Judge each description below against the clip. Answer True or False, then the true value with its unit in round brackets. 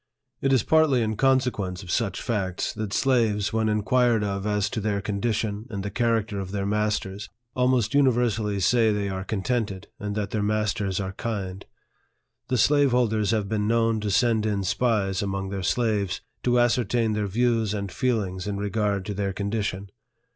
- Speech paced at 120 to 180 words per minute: True (175 wpm)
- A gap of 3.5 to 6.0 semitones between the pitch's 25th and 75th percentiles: False (2.8 semitones)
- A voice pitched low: True (105 Hz)